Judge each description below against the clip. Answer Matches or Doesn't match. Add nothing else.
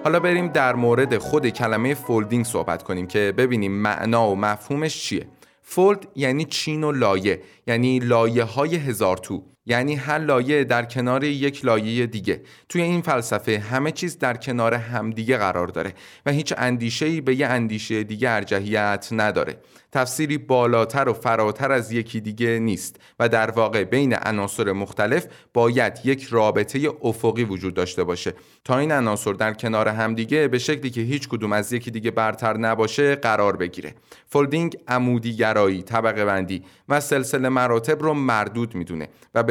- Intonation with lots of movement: Doesn't match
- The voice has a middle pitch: Doesn't match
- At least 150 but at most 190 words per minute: Matches